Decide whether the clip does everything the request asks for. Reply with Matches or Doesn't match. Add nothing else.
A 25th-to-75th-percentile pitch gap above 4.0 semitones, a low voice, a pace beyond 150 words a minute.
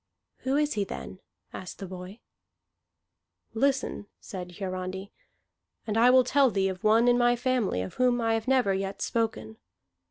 Doesn't match